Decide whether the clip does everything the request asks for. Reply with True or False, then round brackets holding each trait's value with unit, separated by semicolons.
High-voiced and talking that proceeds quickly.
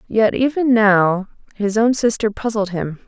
False (215 Hz; 155 wpm)